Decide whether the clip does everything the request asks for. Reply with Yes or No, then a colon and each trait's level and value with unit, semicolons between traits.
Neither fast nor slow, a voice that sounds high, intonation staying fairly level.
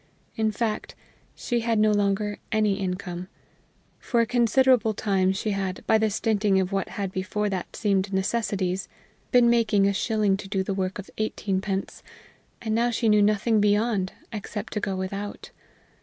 Yes: average, 160 wpm; high, 205 Hz; narrow, 2.2 semitones